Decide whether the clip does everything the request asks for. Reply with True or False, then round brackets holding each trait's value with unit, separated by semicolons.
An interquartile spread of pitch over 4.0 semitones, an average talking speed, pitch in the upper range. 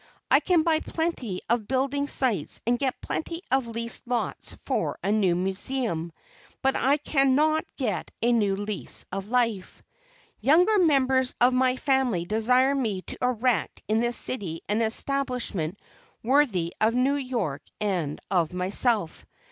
True (5.0 semitones; 145 wpm; 240 Hz)